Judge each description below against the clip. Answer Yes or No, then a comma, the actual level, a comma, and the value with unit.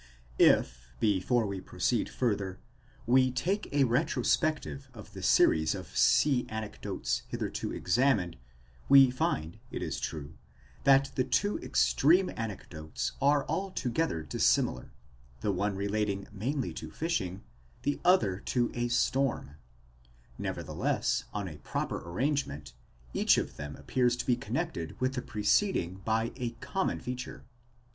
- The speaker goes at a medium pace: No, slow, 130 wpm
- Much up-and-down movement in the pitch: Yes, wide, 6.2 semitones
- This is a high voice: No, low, 120 Hz